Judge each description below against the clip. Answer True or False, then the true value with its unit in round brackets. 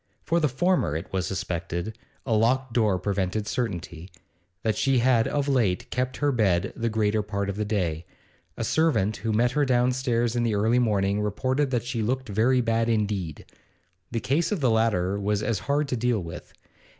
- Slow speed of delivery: False (185 wpm)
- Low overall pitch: True (110 Hz)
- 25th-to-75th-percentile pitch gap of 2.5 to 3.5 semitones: False (4.0 semitones)